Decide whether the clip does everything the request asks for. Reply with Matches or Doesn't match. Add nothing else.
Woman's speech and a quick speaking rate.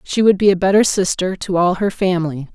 Matches